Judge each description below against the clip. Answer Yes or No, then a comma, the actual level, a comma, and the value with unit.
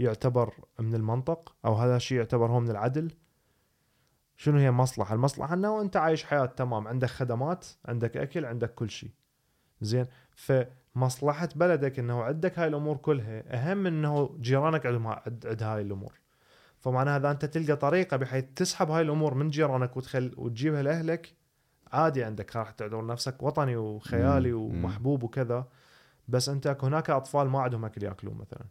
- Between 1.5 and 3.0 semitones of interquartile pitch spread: No, average, 4.1 semitones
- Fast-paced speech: Yes, fast, 155 wpm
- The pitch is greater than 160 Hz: No, low, 130 Hz